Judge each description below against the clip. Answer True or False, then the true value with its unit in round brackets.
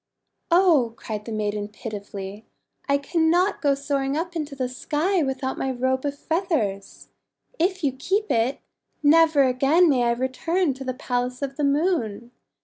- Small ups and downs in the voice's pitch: False (4.8 semitones)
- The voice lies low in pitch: False (275 Hz)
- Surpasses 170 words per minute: False (155 wpm)